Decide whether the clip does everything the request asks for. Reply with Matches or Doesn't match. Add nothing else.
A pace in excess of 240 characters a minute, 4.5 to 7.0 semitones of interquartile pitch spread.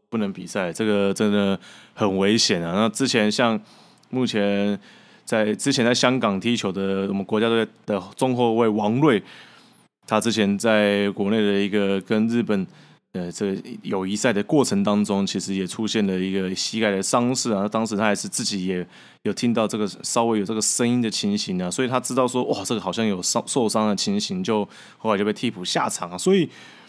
Doesn't match